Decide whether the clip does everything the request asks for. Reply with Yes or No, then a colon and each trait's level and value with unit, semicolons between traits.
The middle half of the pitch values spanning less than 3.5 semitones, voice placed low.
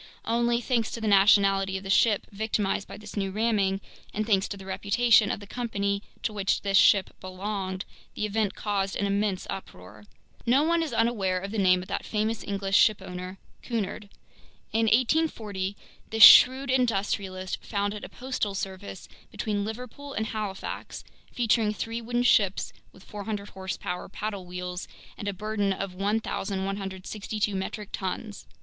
No: narrow, 2.4 semitones; high, 205 Hz